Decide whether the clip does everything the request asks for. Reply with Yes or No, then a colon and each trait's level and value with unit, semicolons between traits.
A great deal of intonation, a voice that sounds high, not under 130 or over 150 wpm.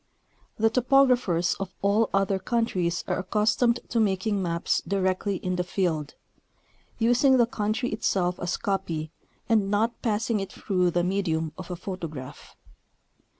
No: average, 3.9 semitones; high, 195 Hz; average, 140 wpm